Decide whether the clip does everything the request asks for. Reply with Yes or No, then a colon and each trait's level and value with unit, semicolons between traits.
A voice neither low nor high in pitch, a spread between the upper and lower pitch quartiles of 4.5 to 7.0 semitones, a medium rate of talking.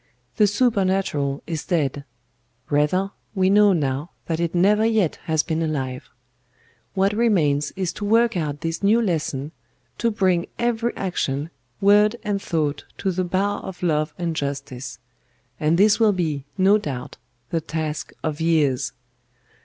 Yes: medium, 170 Hz; average, 5.2 semitones; average, 145 wpm